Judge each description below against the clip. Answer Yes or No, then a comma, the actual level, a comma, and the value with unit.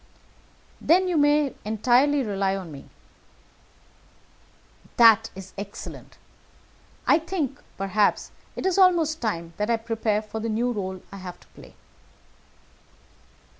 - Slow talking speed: Yes, slow, 125 wpm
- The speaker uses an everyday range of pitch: No, wide, 6.6 semitones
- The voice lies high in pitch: Yes, high, 225 Hz